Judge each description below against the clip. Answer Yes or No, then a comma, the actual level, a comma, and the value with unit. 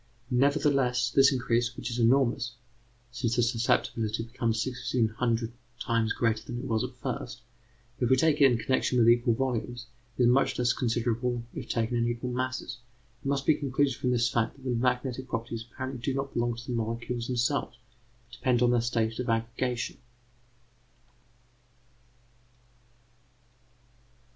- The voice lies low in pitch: Yes, low, 120 Hz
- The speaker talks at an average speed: Yes, average, 155 wpm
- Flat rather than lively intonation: Yes, narrow, 1.7 semitones